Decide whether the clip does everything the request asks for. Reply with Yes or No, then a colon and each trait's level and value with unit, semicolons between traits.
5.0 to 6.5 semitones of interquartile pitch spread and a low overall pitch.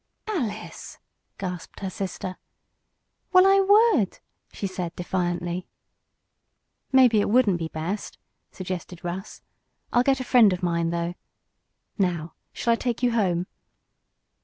No: wide, 5.6 semitones; high, 190 Hz